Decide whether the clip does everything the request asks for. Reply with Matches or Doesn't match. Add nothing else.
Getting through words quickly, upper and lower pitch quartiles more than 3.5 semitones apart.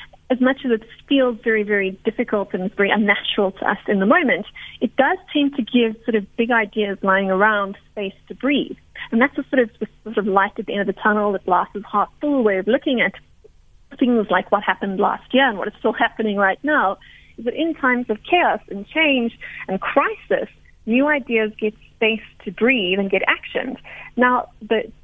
Matches